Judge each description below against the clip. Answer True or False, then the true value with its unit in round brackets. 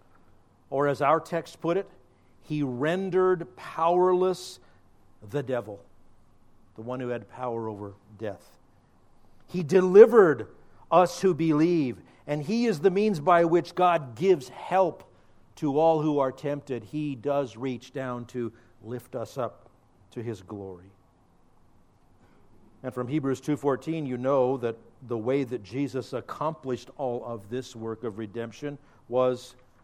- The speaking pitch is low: True (125 Hz)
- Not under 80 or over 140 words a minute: True (135 wpm)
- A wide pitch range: True (5.7 semitones)